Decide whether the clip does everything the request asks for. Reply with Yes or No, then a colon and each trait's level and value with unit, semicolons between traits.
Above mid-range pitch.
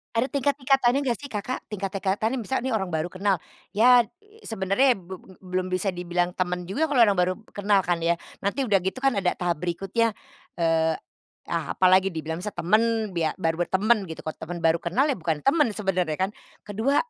Yes: high, 195 Hz